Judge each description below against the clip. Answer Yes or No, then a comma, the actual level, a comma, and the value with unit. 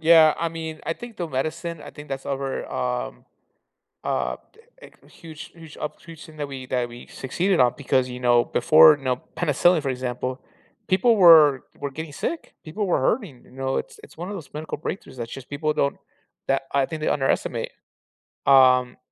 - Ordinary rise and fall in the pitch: Yes, average, 4.0 semitones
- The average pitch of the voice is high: No, medium, 145 Hz